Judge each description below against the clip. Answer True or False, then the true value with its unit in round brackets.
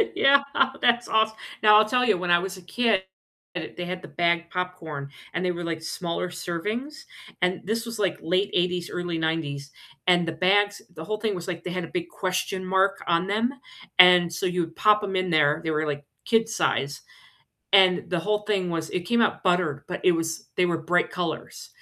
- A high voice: False (180 Hz)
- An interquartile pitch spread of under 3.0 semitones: False (3.3 semitones)